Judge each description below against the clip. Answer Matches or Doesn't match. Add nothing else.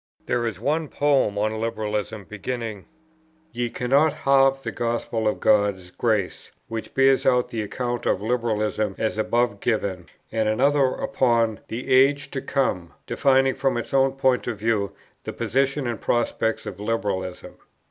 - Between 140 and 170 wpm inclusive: Matches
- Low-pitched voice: Matches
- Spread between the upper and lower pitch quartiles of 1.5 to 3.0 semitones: Doesn't match